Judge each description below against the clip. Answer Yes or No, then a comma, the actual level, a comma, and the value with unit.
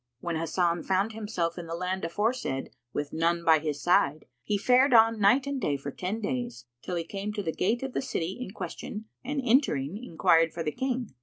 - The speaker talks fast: Yes, fast, 210 wpm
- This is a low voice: No, medium, 185 Hz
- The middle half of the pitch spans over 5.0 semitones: Yes, wide, 5.6 semitones